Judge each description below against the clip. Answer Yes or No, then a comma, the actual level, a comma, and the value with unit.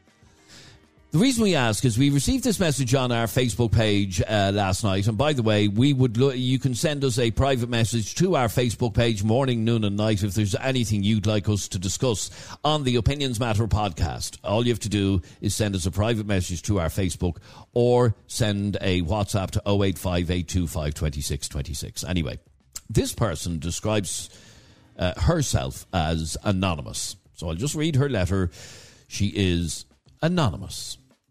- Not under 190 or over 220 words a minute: No, average, 170 wpm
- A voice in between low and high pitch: No, low, 105 Hz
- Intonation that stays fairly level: No, average, 4.6 semitones